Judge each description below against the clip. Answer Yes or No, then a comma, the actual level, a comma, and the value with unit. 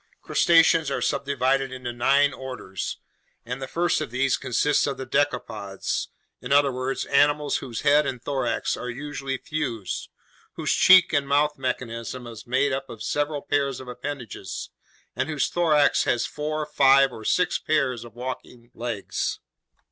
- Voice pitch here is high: No, low, 135 Hz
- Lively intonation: No, average, 2.8 semitones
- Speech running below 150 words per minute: No, average, 155 wpm